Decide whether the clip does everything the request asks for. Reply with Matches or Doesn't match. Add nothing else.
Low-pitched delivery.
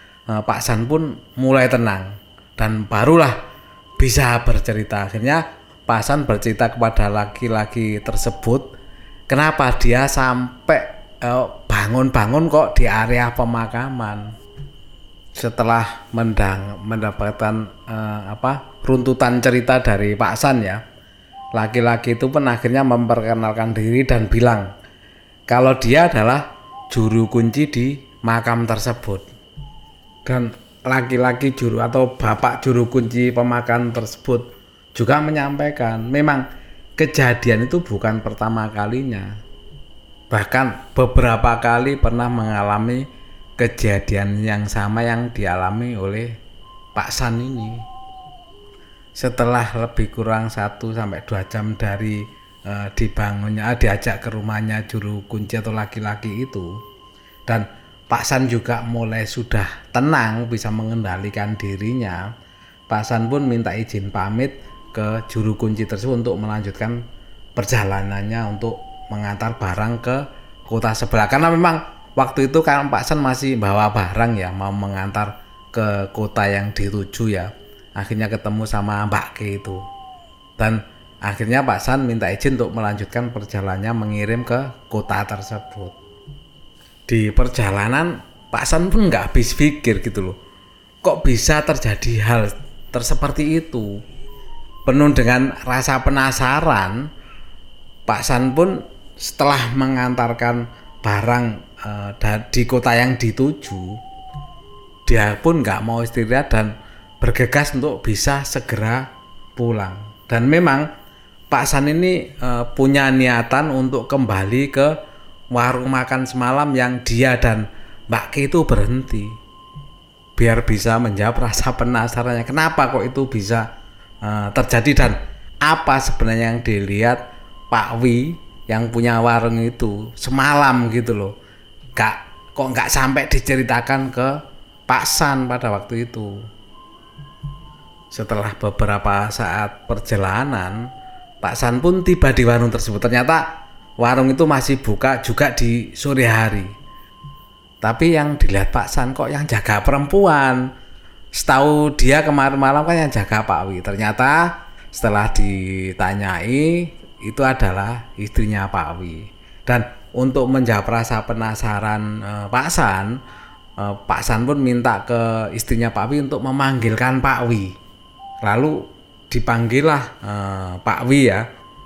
Matches